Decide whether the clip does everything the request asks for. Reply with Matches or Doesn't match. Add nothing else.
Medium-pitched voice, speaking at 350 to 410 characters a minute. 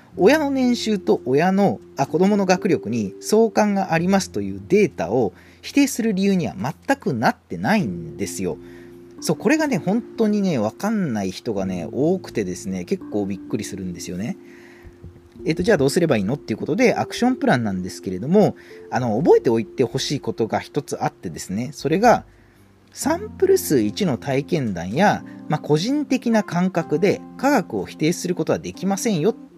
Matches